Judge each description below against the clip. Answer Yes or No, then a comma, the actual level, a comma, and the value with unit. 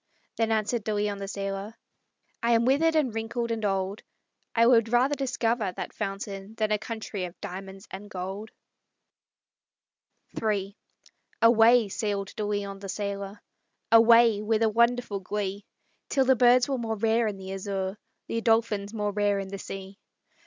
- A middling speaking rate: Yes, average, 160 wpm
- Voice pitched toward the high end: Yes, high, 210 Hz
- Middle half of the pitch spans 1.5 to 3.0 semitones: Yes, narrow, 2.6 semitones